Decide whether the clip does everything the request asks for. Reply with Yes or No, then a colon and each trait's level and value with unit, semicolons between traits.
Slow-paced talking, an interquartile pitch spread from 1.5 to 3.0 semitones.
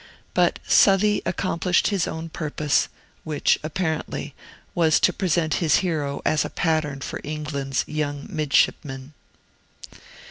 Yes: slow, 115 wpm; narrow, 2.6 semitones